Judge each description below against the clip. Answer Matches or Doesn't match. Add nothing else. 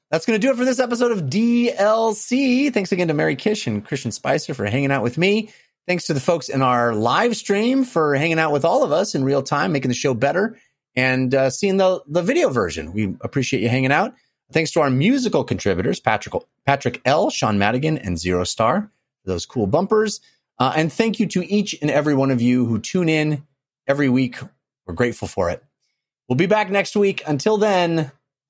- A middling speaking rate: Doesn't match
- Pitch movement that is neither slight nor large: Doesn't match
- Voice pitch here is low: Doesn't match